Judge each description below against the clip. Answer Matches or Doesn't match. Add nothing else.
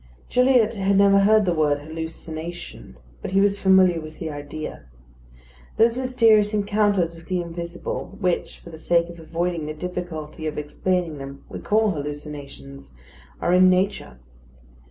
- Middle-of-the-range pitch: Matches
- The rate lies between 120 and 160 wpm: Matches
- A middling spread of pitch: Matches